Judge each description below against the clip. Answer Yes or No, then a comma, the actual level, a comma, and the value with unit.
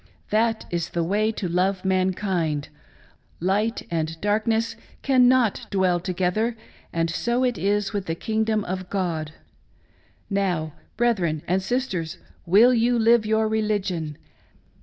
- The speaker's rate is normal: No, slow, 130 wpm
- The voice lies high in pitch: Yes, high, 195 Hz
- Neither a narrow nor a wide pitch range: Yes, average, 4.1 semitones